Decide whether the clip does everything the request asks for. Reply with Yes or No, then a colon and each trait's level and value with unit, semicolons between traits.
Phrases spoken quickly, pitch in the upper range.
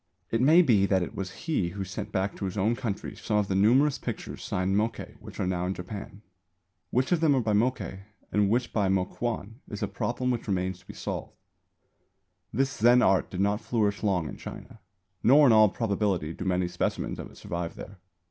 No: fast, 210 wpm; low, 105 Hz